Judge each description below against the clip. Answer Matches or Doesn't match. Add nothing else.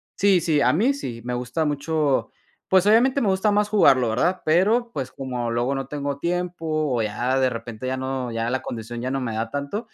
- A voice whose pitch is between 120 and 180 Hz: Matches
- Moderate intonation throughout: Doesn't match